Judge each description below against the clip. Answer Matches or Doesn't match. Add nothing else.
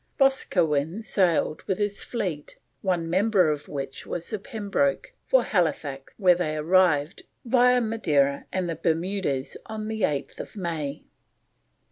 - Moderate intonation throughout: Doesn't match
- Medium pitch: Matches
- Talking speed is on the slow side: Matches